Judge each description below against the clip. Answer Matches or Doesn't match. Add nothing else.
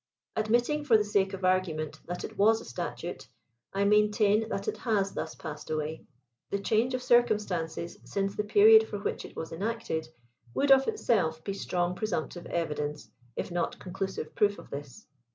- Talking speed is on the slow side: Doesn't match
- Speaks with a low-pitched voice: Doesn't match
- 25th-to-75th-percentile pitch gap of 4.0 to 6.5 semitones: Matches